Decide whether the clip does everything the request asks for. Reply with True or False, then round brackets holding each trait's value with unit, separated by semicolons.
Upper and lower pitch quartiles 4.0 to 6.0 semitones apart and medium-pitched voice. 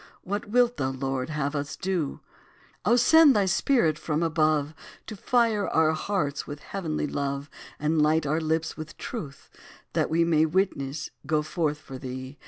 True (4.8 semitones; 155 Hz)